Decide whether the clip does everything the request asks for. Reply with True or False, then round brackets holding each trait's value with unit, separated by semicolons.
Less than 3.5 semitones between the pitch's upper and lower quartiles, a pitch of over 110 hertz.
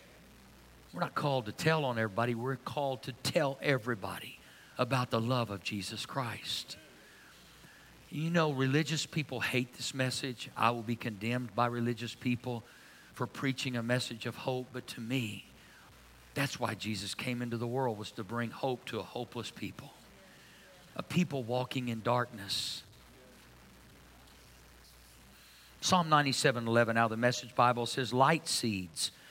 True (2.9 semitones; 120 Hz)